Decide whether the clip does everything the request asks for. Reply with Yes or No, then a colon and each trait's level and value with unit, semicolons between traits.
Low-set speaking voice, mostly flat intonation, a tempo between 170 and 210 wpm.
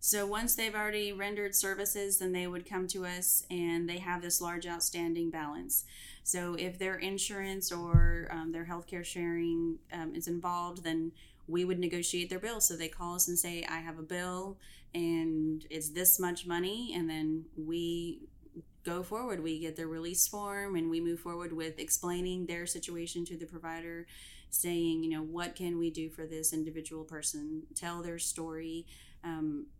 No: medium, 170 Hz; narrow, 1.7 semitones; average, 175 wpm